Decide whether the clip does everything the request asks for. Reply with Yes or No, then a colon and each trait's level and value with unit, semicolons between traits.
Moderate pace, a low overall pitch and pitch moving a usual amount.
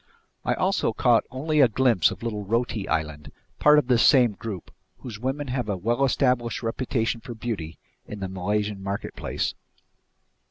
Yes: average, 160 wpm; low, 115 Hz; average, 3.9 semitones